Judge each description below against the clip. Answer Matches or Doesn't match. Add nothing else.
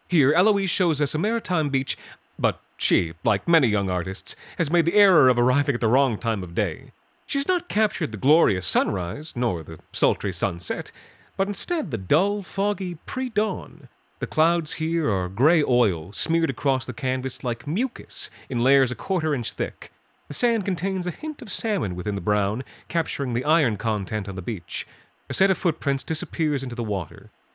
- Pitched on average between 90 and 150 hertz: Matches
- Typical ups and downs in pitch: Doesn't match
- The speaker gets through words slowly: Doesn't match